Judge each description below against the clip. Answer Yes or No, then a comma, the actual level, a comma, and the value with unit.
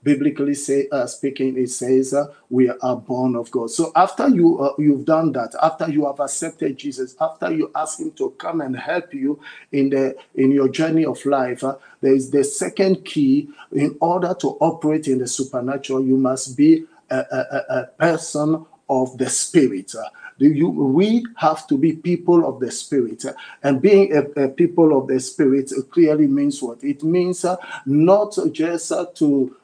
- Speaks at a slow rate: No, average, 185 wpm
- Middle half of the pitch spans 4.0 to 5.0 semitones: Yes, average, 4.7 semitones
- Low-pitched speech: No, medium, 150 Hz